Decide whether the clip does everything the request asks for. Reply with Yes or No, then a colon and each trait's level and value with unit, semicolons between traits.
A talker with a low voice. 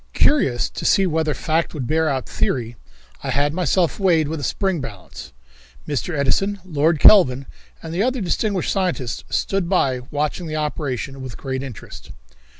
No: medium, 155 Hz